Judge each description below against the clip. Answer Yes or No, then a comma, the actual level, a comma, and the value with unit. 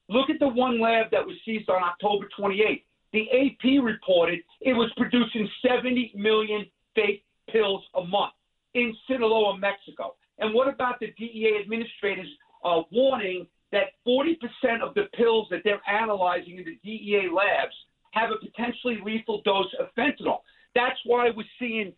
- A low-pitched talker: No, high, 220 Hz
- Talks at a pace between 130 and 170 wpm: Yes, average, 160 wpm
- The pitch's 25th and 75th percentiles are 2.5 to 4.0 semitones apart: Yes, average, 3.4 semitones